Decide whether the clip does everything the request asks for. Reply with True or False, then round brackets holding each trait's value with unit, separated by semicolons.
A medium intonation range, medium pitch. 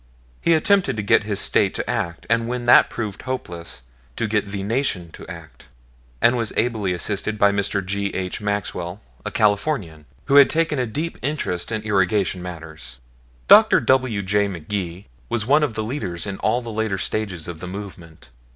False (4.6 semitones; 105 Hz)